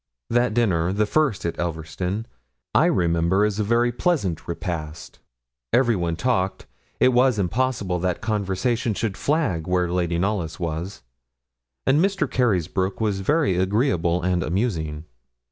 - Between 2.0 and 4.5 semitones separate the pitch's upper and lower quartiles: No, wide, 5.4 semitones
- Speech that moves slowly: Yes, slow, 130 wpm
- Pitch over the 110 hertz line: No, very low, 95 Hz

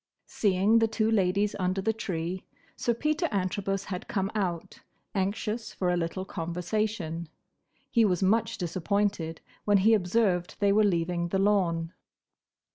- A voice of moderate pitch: No, high, 195 Hz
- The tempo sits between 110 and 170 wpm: Yes, average, 140 wpm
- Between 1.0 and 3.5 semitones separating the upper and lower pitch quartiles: Yes, average, 3.2 semitones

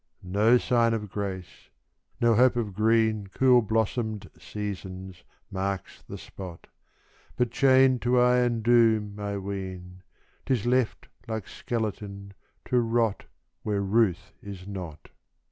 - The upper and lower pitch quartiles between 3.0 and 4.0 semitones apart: Yes, average, 3.3 semitones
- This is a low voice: Yes, low, 105 Hz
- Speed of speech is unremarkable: No, slow, 120 wpm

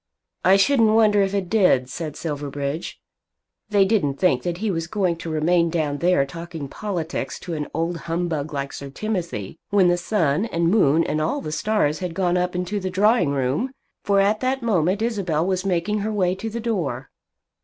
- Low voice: No, medium, 175 Hz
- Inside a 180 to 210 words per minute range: Yes, average, 190 wpm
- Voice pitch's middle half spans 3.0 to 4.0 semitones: No, average, 4.7 semitones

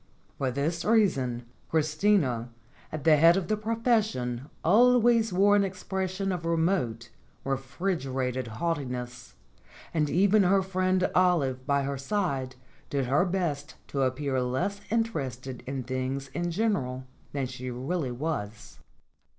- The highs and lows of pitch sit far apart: Yes, wide, 6.6 semitones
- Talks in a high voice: No, medium, 150 Hz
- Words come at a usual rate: No, slow, 130 wpm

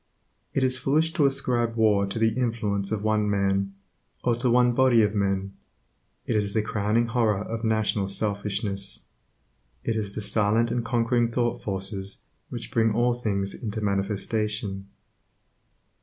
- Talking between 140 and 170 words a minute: Yes, average, 150 wpm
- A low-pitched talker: Yes, low, 110 Hz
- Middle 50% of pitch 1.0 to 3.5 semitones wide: Yes, average, 2.8 semitones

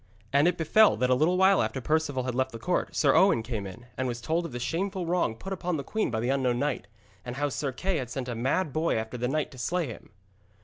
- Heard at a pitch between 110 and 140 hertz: Yes, low, 135 Hz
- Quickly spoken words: Yes, fast, 265 wpm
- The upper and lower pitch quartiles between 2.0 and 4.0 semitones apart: No, wide, 5.5 semitones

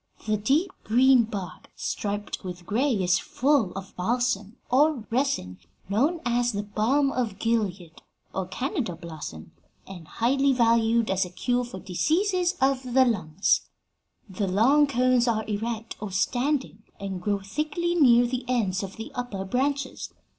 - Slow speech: No, average, 145 wpm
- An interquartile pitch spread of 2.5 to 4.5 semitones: No, average, 5.2 semitones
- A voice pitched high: Yes, high, 230 Hz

